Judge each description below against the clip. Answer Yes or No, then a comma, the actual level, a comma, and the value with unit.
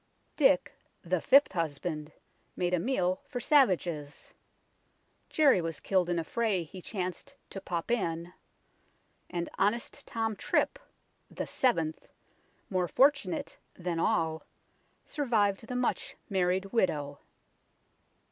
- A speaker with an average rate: No, slow, 125 wpm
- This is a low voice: No, medium, 185 Hz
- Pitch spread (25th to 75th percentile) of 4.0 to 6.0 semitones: Yes, wide, 5.4 semitones